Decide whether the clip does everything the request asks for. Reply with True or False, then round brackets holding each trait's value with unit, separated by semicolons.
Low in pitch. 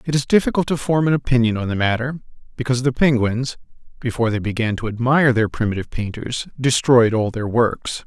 True (120 Hz)